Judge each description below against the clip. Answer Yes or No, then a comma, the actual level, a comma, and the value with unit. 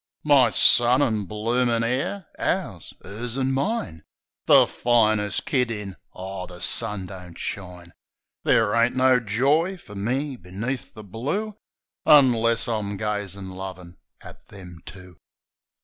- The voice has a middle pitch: No, low, 110 Hz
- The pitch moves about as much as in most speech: Yes, average, 4.8 semitones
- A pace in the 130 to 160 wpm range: Yes, slow, 135 wpm